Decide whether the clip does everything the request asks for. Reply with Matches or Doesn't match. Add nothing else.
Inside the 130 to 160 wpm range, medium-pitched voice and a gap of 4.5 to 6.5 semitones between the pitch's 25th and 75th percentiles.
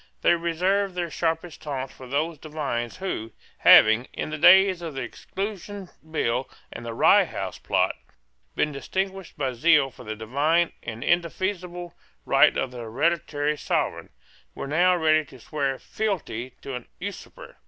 Matches